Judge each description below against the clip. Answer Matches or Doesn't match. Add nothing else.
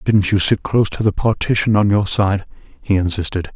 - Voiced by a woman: Doesn't match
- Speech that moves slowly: Doesn't match